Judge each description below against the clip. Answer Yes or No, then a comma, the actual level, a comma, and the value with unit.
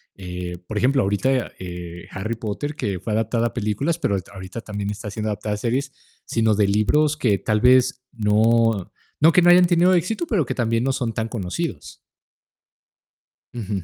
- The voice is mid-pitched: No, low, 115 Hz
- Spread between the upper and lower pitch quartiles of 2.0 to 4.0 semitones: No, average, 4.5 semitones